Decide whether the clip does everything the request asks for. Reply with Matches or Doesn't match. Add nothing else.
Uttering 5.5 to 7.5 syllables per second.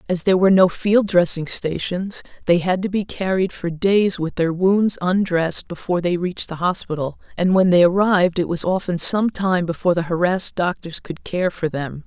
Doesn't match